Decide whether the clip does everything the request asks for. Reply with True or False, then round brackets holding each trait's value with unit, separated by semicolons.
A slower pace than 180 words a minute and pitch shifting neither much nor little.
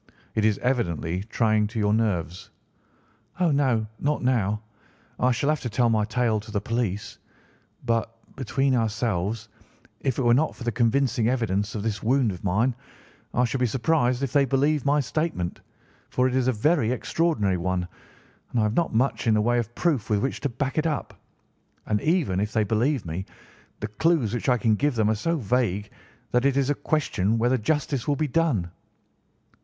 False (190 wpm; 4.3 semitones)